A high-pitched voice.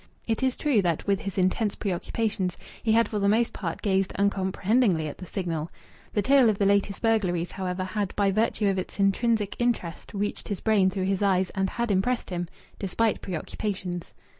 Yes: high, 200 Hz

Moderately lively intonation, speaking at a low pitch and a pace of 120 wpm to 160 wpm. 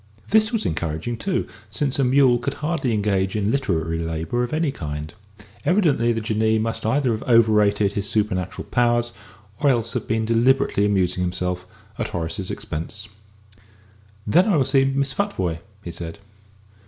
No: wide, 6.4 semitones; low, 110 Hz; average, 155 wpm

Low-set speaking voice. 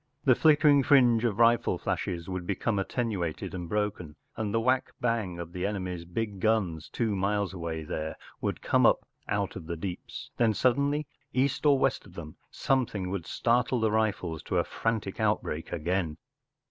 Yes: low, 105 Hz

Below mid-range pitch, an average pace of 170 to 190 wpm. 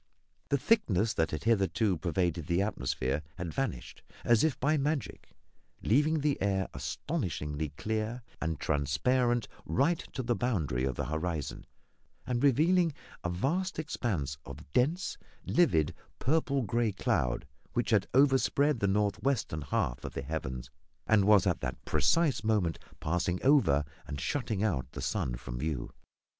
No: low, 105 Hz; average, 145 wpm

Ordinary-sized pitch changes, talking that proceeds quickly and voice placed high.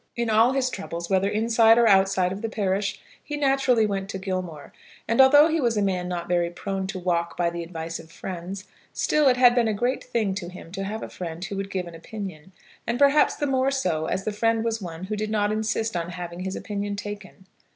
Yes: average, 4.1 semitones; fast, 235 wpm; high, 200 Hz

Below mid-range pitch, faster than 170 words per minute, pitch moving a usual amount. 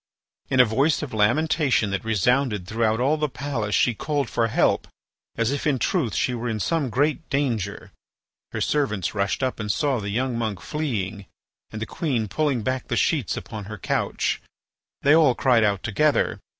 Yes: low, 120 Hz; average, 180 wpm; average, 4.8 semitones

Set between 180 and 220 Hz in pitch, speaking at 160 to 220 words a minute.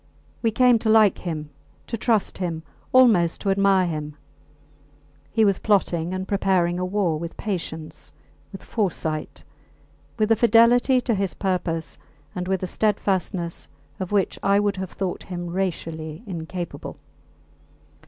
No: high, 190 Hz; average, 140 wpm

